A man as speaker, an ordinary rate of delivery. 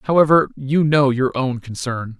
Yes: male; average, 165 wpm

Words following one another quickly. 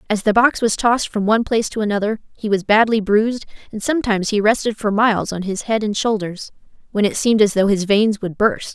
Yes: fast, 235 wpm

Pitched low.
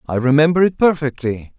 No: medium, 145 Hz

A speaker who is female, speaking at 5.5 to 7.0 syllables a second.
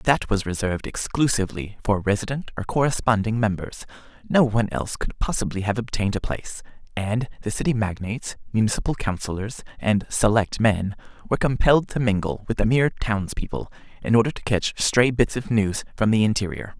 No: male; 5.8 syllables/s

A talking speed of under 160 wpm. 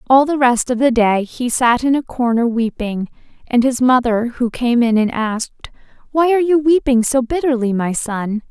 No: average, 190 wpm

